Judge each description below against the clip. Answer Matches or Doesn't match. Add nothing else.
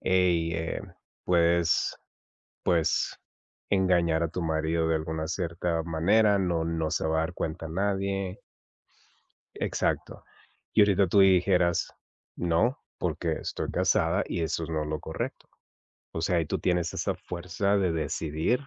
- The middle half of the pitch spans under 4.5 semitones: Matches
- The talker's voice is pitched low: Matches